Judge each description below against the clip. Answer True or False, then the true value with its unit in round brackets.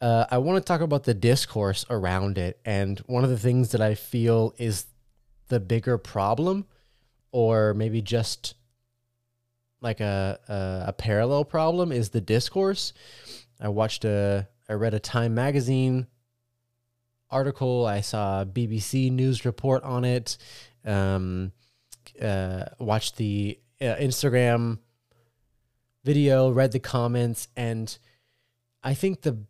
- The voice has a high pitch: False (120 Hz)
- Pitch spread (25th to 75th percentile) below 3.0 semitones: True (2.6 semitones)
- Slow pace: True (130 wpm)